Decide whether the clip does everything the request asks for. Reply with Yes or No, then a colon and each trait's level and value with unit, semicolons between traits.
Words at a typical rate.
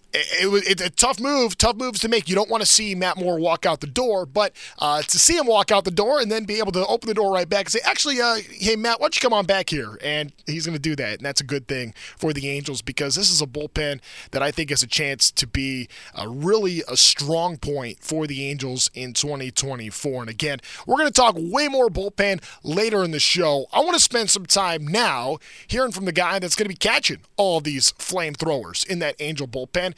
No: fast, 250 wpm